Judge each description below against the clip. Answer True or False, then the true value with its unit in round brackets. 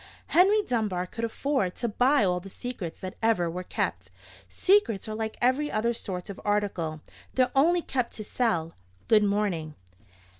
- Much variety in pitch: True (5.7 semitones)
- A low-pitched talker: False (215 Hz)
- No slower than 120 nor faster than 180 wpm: True (160 wpm)